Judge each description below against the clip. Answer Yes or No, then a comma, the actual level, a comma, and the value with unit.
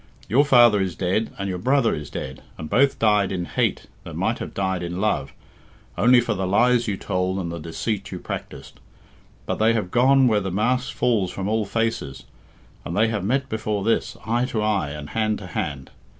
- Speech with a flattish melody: No, average, 4.1 semitones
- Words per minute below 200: No, fast, 205 wpm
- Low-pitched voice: Yes, low, 105 Hz